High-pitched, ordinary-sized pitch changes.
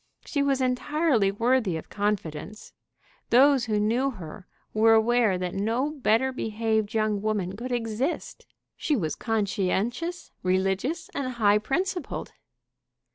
Yes: high, 225 Hz; average, 4.3 semitones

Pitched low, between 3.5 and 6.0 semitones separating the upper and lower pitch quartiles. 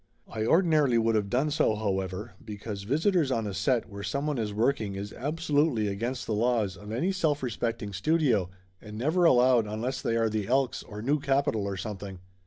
Yes: low, 115 Hz; average, 5.0 semitones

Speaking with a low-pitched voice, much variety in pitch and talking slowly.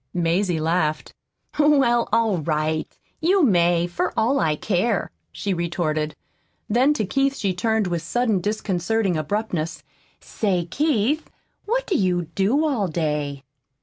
No: high, 190 Hz; wide, 5.9 semitones; slow, 130 wpm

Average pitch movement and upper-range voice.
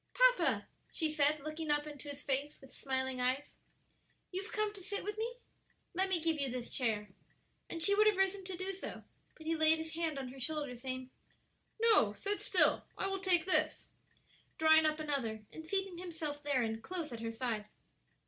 No: wide, 5.9 semitones; very high, 310 Hz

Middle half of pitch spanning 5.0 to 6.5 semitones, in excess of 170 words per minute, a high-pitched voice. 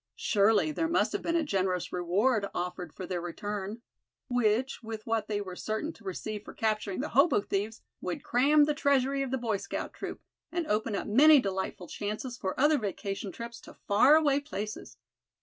Yes: average, 5.3 semitones; average, 185 wpm; high, 220 Hz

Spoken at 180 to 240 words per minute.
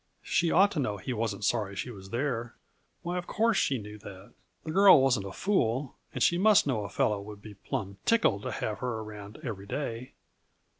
Yes: fast, 205 wpm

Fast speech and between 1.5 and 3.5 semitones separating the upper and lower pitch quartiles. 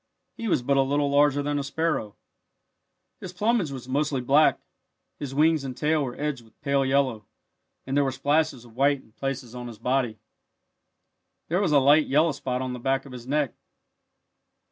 No: average, 190 wpm; narrow, 2.6 semitones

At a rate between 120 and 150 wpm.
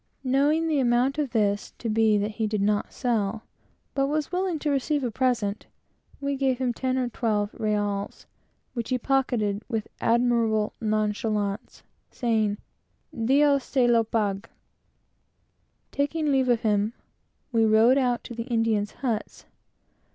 Yes: average, 145 wpm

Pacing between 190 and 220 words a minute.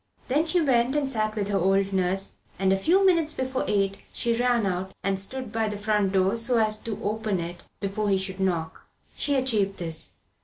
Yes: fast, 205 wpm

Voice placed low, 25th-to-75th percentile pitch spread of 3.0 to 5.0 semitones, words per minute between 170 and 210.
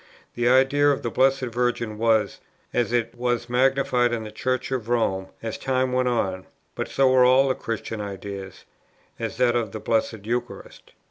No: low, 120 Hz; narrow, 2.5 semitones; average, 180 wpm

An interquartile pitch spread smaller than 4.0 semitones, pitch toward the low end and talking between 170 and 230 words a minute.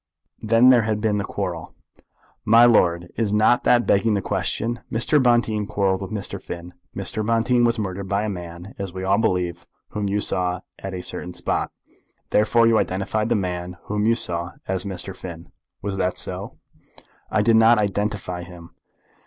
Yes: average, 3.5 semitones; low, 100 Hz; average, 175 wpm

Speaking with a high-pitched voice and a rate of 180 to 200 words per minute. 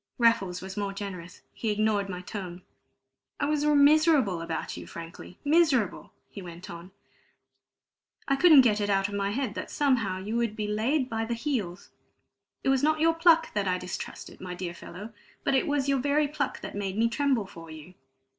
Yes: high, 215 Hz; average, 190 wpm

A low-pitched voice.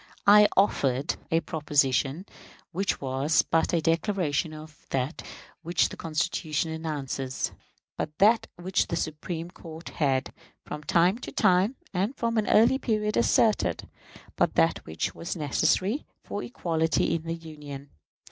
No: medium, 165 Hz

